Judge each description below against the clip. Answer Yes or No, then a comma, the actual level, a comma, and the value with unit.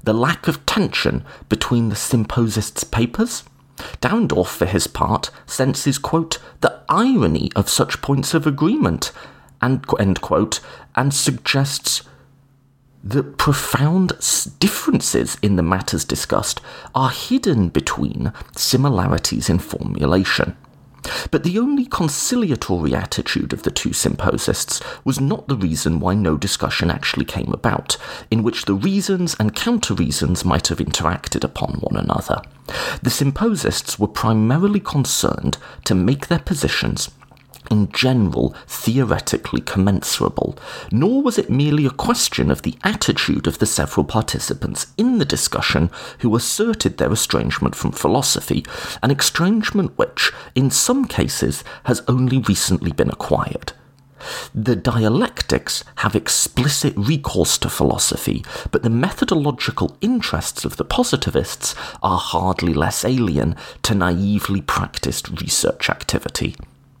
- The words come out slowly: Yes, slow, 125 wpm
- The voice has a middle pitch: No, low, 130 Hz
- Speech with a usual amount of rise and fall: No, wide, 8.1 semitones